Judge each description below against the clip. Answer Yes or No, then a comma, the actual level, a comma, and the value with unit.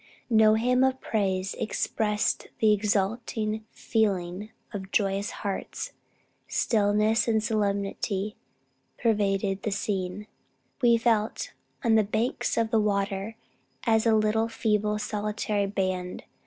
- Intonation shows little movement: Yes, narrow, 1.9 semitones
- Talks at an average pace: No, slow, 115 wpm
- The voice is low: No, high, 210 Hz